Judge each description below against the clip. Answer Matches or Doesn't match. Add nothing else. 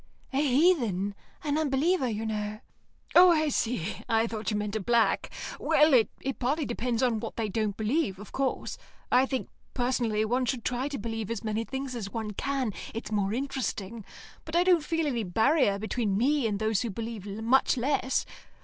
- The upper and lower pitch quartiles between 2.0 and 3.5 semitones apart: Doesn't match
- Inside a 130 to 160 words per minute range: Doesn't match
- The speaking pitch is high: Matches